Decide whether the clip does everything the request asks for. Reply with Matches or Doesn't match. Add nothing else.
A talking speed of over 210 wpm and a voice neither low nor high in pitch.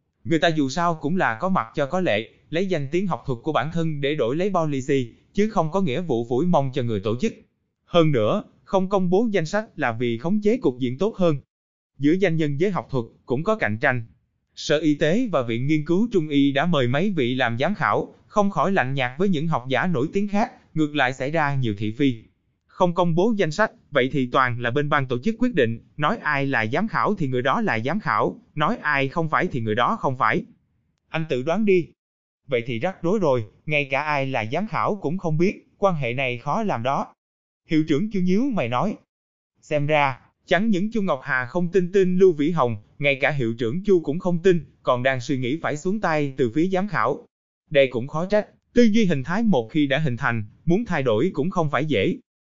Matches